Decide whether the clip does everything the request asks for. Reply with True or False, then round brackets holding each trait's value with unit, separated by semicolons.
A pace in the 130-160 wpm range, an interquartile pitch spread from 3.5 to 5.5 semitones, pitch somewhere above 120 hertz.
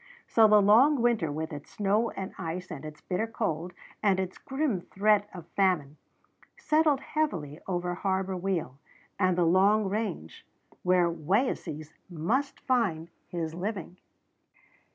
True (135 wpm; 4.4 semitones; 190 Hz)